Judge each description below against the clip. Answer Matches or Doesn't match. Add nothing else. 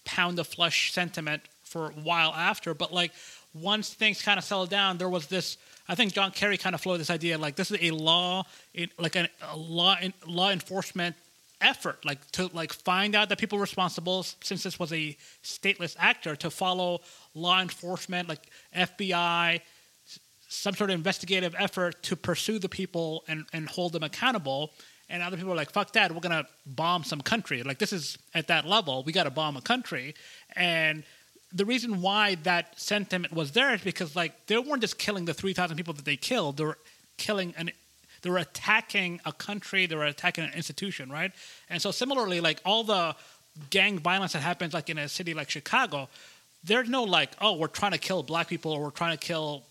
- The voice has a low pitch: Doesn't match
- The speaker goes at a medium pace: Matches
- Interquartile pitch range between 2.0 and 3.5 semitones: Matches